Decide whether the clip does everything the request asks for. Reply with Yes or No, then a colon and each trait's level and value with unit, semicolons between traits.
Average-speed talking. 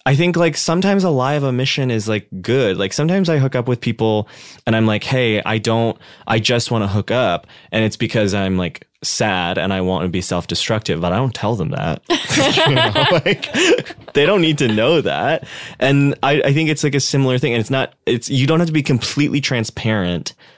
No: fast, 230 wpm